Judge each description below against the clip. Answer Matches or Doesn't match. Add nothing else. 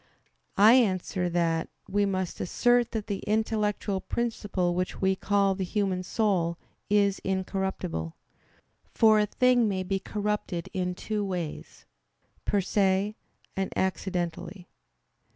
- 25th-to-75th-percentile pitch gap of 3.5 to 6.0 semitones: Doesn't match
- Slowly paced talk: Matches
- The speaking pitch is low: Doesn't match